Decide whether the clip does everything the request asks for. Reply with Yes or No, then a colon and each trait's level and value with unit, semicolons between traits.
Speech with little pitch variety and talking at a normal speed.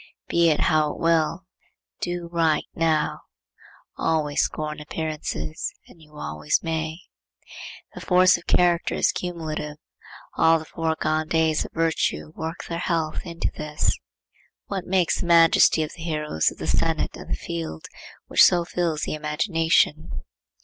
Yes: narrow, 1.8 semitones; average, 145 wpm